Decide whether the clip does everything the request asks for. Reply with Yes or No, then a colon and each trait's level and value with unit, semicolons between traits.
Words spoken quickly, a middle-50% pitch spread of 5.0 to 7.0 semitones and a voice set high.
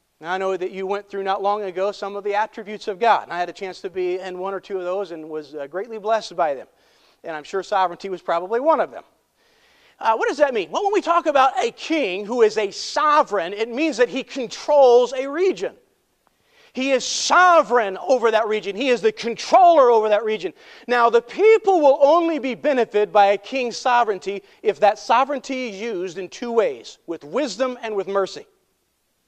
Yes: fast, 215 wpm; wide, 5.6 semitones; high, 220 Hz